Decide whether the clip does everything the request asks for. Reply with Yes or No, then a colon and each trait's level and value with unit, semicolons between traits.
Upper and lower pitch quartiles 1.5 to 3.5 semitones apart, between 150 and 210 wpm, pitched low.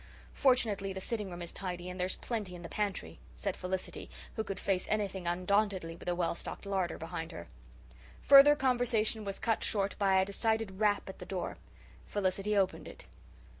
No: average, 2.8 semitones; average, 180 wpm; high, 195 Hz